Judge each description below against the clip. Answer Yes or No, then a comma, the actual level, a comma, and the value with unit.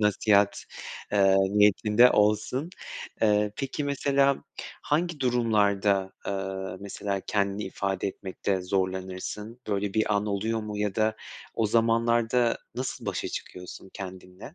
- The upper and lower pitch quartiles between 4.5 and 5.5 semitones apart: No, average, 2.9 semitones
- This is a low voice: Yes, low, 105 Hz